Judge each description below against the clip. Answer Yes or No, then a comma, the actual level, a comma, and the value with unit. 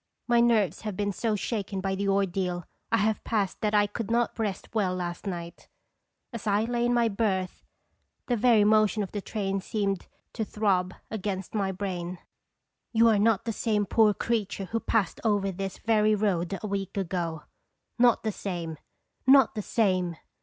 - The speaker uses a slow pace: No, average, 175 wpm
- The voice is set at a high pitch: Yes, high, 205 Hz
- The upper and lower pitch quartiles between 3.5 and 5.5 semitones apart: No, narrow, 2.6 semitones